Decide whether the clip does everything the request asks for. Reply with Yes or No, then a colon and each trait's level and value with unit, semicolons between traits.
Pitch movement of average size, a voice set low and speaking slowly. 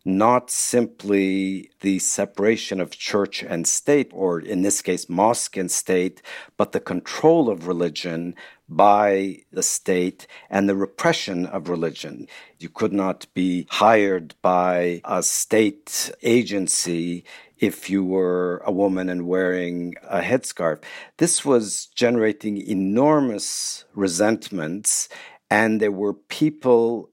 Yes: average, 3.2 semitones; very low, 95 Hz; slow, 120 wpm